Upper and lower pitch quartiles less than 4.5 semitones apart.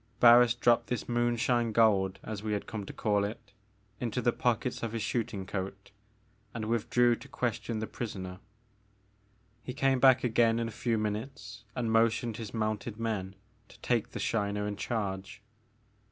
Yes: narrow, 2.6 semitones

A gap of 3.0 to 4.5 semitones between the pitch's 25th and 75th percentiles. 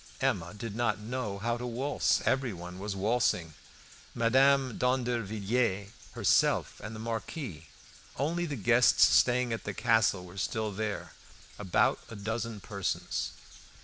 Yes: average, 3.6 semitones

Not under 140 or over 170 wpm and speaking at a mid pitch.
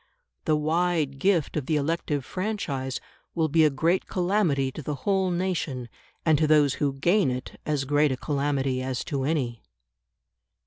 Yes: average, 165 wpm; medium, 150 Hz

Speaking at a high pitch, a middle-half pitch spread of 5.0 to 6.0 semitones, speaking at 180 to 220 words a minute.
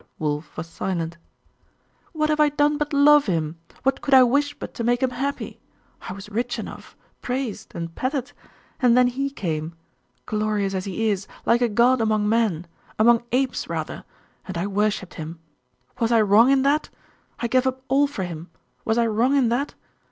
Yes: high, 235 Hz; average, 5.3 semitones; average, 185 wpm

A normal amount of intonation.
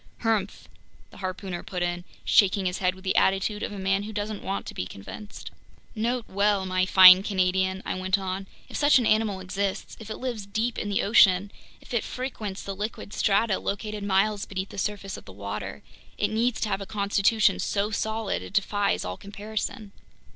No: narrow, 2.2 semitones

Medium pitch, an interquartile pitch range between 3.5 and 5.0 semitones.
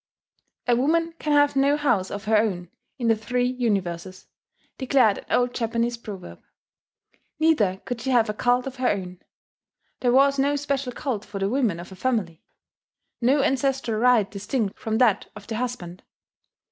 No: high, 240 Hz; average, 4.6 semitones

